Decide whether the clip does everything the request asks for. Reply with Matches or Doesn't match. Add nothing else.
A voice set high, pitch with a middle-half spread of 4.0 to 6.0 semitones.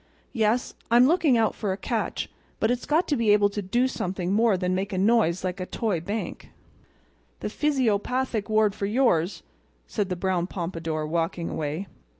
Matches